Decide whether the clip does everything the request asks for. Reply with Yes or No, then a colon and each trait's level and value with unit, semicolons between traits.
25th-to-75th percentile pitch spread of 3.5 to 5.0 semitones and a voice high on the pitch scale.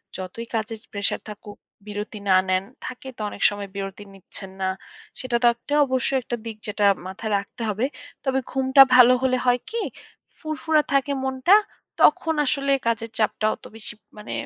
Yes: average, 4.3 semitones; high, 230 Hz